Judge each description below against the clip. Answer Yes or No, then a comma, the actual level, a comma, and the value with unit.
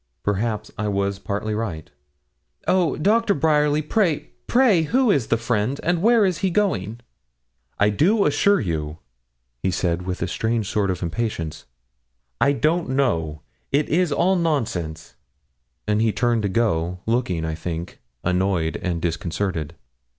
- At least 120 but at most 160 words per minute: Yes, average, 145 wpm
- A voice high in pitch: No, low, 110 Hz